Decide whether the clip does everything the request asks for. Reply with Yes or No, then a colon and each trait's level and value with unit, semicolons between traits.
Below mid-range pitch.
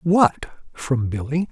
No: medium, 150 Hz